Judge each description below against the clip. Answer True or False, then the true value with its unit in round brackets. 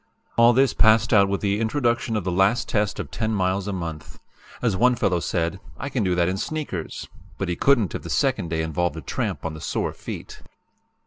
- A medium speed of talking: False (215 wpm)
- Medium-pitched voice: False (100 Hz)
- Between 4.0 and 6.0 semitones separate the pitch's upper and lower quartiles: True (4.8 semitones)